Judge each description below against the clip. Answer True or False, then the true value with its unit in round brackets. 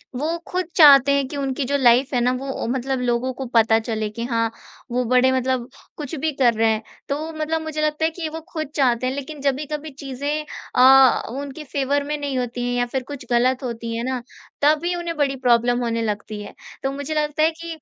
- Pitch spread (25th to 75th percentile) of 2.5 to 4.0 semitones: True (3.5 semitones)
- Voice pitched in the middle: False (270 Hz)